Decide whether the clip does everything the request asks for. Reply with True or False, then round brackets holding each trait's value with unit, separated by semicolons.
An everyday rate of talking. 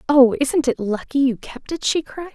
False (230 wpm)